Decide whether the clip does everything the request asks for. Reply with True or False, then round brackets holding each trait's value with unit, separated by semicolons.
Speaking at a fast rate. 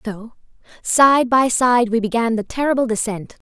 False (155 wpm)